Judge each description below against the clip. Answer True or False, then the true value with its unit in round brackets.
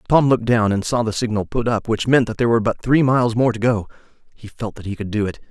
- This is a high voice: False (115 Hz)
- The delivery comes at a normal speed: False (295 wpm)